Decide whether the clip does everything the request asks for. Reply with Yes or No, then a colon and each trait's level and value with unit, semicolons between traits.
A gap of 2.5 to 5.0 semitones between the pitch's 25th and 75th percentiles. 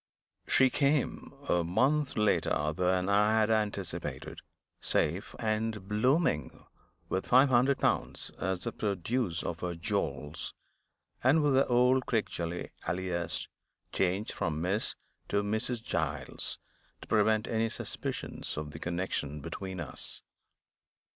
No: wide, 5.4 semitones